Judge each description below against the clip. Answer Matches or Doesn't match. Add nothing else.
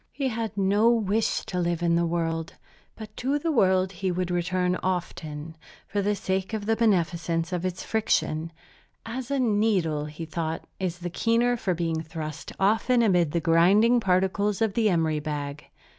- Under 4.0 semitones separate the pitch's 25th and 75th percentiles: Doesn't match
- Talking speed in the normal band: Matches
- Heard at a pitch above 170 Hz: Matches